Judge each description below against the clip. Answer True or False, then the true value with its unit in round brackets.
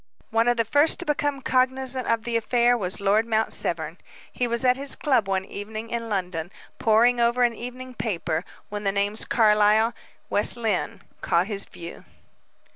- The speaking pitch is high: True (225 Hz)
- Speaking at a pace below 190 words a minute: True (175 wpm)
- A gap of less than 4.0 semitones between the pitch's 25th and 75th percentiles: True (3.3 semitones)